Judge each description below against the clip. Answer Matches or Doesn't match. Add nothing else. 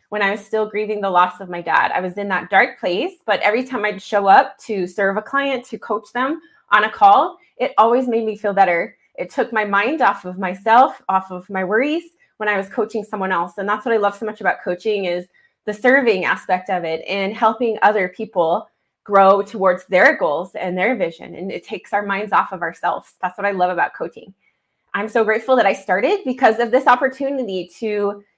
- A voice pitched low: Doesn't match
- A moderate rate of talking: Doesn't match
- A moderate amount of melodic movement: Matches